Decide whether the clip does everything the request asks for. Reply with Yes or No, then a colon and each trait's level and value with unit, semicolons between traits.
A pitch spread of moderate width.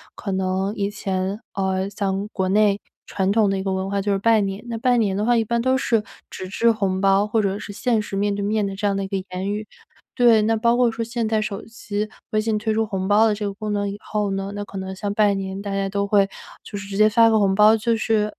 No: narrow, 2.0 semitones